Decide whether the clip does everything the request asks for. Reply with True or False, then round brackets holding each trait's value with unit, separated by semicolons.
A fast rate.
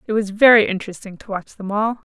True (230 wpm)